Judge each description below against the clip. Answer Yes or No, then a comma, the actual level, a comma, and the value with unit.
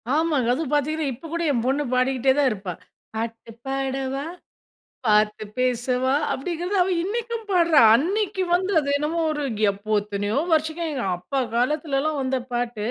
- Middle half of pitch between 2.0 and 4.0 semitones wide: No, average, 4.7 semitones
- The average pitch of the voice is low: No, very high, 270 Hz